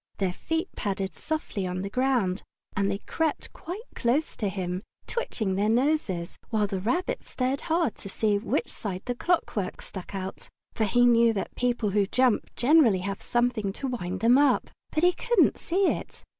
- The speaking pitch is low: No, high, 225 Hz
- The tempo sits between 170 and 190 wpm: Yes, average, 180 wpm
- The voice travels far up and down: Yes, wide, 5.7 semitones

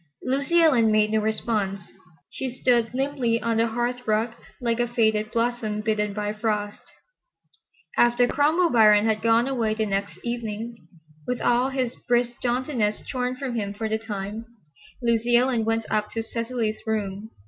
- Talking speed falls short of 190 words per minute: Yes, average, 160 wpm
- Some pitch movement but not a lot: No, narrow, 2.3 semitones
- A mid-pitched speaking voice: No, high, 230 Hz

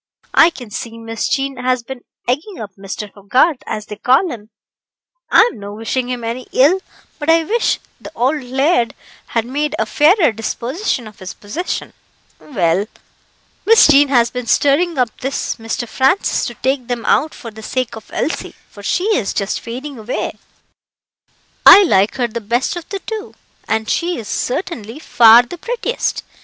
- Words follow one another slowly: No, average, 170 wpm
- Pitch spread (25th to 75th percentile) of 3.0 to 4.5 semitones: No, average, 5.1 semitones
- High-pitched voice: Yes, very high, 250 Hz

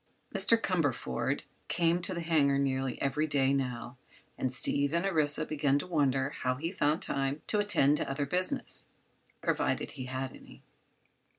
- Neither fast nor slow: Yes, average, 155 wpm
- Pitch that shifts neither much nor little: Yes, average, 3.6 semitones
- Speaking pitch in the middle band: Yes, medium, 145 Hz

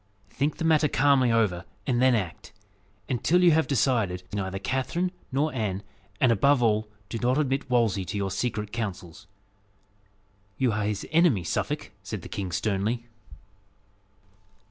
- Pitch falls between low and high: No, low, 115 Hz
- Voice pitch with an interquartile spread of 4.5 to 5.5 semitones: Yes, average, 5.2 semitones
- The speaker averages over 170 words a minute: No, average, 155 wpm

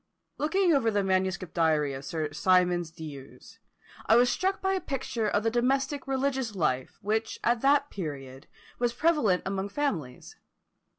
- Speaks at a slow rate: No, average, 155 wpm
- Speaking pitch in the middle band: No, high, 210 Hz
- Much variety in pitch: Yes, wide, 8.5 semitones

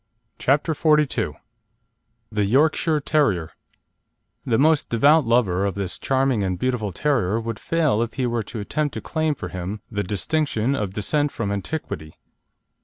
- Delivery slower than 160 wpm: Yes, average, 150 wpm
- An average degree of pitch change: No, wide, 6.5 semitones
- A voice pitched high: No, low, 120 Hz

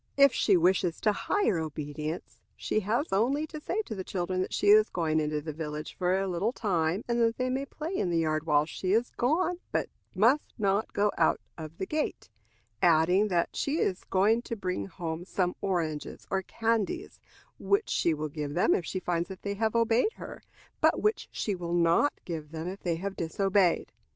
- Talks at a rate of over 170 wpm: Yes, average, 200 wpm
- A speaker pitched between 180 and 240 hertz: Yes, high, 190 Hz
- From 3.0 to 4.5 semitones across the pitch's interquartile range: No, wide, 5.6 semitones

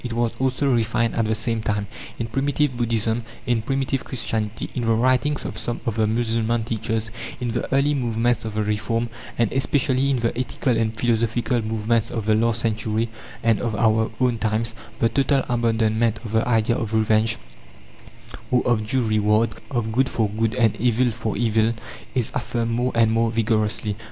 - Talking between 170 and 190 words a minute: Yes, average, 180 wpm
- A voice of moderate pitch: No, low, 115 Hz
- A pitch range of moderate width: No, narrow, 1.7 semitones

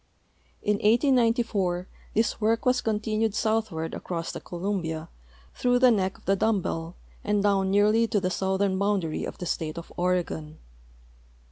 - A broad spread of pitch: No, average, 3.8 semitones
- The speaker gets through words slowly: No, average, 155 wpm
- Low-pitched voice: No, high, 200 Hz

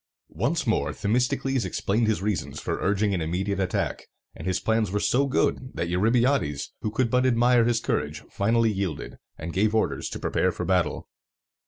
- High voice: No, low, 110 Hz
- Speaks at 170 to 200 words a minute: Yes, average, 175 wpm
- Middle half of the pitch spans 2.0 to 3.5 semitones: No, average, 4.1 semitones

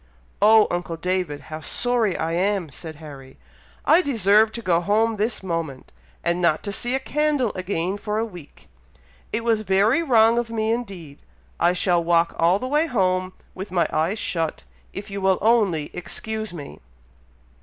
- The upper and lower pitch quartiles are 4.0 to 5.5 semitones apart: Yes, average, 4.7 semitones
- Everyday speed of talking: Yes, average, 170 wpm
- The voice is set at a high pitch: Yes, high, 195 Hz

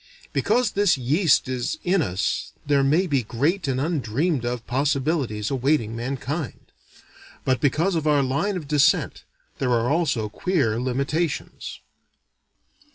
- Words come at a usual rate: No, slow, 130 wpm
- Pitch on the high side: No, medium, 140 Hz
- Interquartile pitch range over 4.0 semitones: Yes, average, 4.6 semitones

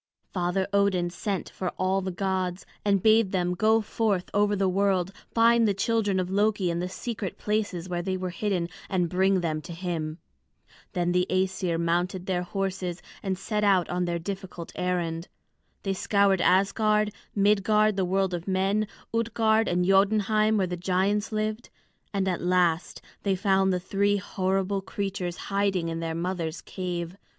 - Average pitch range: No, narrow, 2.3 semitones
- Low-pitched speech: No, high, 190 Hz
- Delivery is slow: No, average, 165 wpm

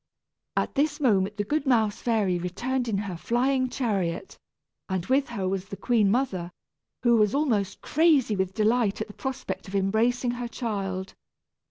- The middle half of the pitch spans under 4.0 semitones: No, average, 4.4 semitones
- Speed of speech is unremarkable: Yes, average, 165 wpm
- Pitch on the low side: No, high, 220 Hz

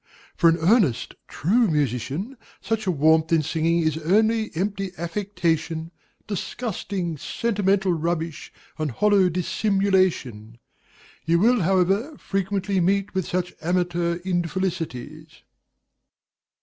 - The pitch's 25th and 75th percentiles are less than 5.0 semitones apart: Yes, average, 3.6 semitones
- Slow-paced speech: Yes, slow, 105 wpm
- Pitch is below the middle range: No, medium, 180 Hz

